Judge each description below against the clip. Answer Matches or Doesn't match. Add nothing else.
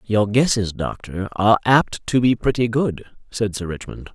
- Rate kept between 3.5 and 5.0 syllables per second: Matches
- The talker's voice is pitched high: Doesn't match